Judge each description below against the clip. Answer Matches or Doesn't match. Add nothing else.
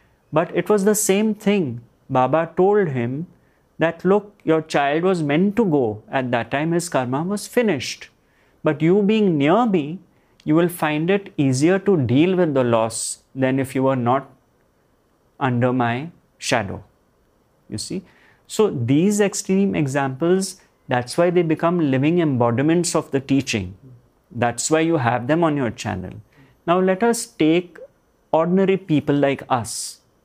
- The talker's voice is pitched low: Doesn't match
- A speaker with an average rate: Matches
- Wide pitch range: Matches